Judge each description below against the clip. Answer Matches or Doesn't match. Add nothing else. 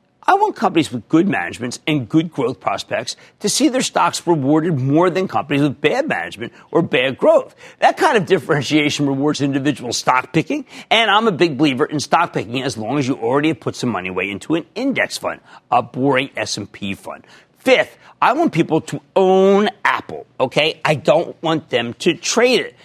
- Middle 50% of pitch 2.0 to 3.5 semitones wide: Doesn't match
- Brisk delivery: Doesn't match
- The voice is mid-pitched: Matches